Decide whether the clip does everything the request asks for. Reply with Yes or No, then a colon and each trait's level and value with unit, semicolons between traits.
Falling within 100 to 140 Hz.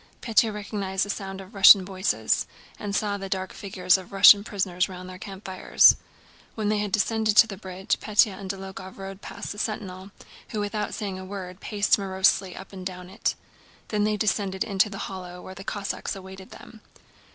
No: high, 195 Hz